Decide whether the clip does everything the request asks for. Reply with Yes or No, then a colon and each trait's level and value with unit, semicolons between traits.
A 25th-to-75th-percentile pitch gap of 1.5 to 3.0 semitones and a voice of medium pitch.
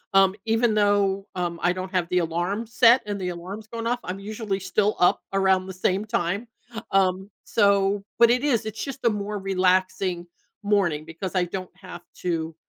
No: narrow, 2.6 semitones; high, 195 Hz